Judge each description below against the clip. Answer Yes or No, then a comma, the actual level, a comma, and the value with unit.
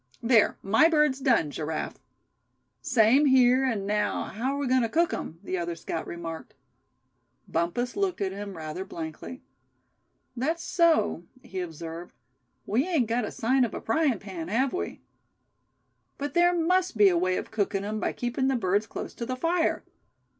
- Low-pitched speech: No, high, 230 Hz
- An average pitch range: No, wide, 6.5 semitones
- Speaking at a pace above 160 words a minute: Yes, average, 170 wpm